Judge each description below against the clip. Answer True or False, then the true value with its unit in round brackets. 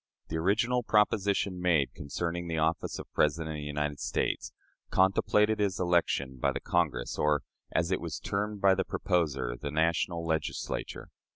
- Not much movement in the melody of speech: False (4.1 semitones)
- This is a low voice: True (85 Hz)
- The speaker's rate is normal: True (160 wpm)